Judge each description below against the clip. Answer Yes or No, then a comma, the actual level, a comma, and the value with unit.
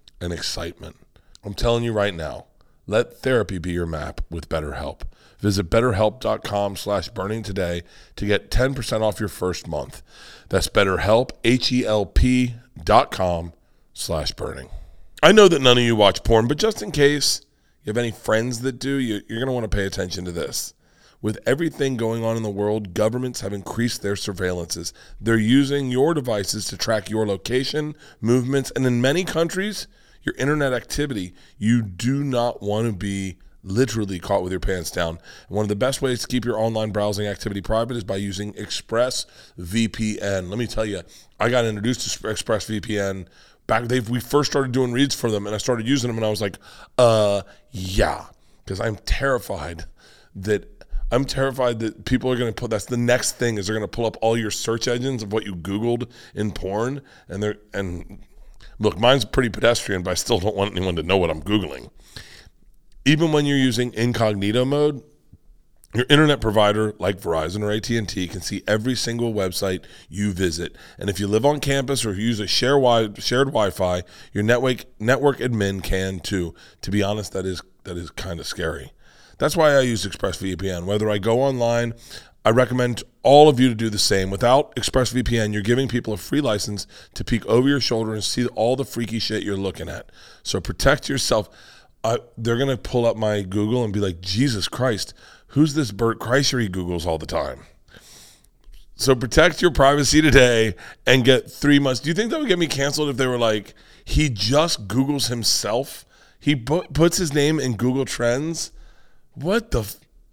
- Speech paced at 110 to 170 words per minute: No, average, 185 wpm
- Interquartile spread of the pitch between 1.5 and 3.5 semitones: No, average, 4.2 semitones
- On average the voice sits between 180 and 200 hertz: No, low, 110 Hz